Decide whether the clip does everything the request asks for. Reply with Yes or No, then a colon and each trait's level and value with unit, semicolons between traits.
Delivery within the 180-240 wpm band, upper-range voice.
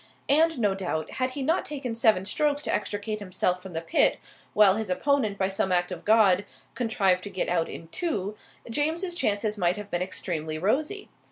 Yes: average, 190 wpm; high, 205 Hz